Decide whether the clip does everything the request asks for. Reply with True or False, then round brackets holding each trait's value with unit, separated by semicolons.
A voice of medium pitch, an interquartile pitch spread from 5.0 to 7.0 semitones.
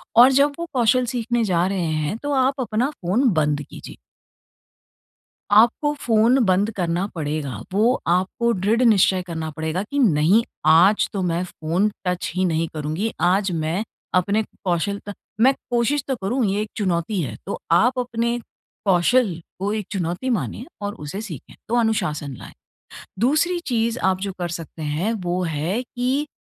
False (200 Hz; 5.5 semitones)